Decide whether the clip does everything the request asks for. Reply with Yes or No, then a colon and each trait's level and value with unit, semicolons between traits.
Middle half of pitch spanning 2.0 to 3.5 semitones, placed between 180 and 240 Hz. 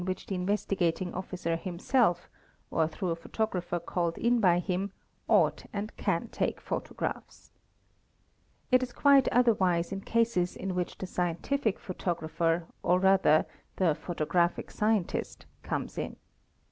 Yes: average, 3.2 semitones; medium, 185 Hz